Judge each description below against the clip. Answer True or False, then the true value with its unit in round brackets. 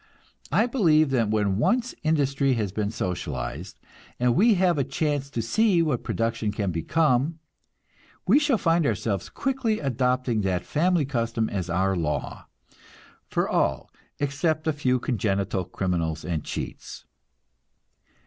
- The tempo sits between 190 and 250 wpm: False (135 wpm)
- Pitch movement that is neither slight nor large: False (7.9 semitones)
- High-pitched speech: False (125 Hz)